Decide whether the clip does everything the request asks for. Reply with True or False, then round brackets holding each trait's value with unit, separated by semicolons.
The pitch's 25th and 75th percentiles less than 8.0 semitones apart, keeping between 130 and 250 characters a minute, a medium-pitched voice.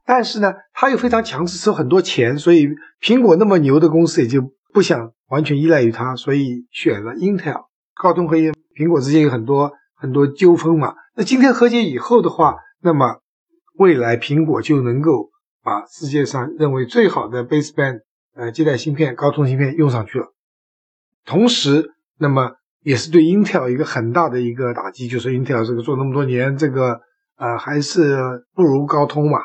False (5.3 semitones; 305 characters per minute; 150 Hz)